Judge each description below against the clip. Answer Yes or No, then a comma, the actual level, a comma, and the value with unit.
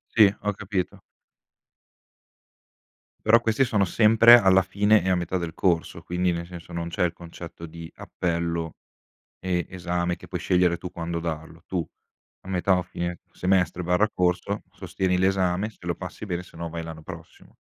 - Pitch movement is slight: Yes, narrow, 2.1 semitones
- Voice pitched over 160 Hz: No, very low, 90 Hz